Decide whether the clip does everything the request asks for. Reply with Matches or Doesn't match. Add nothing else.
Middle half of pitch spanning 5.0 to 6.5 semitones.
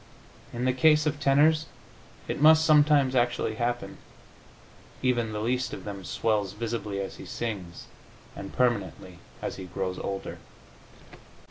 Matches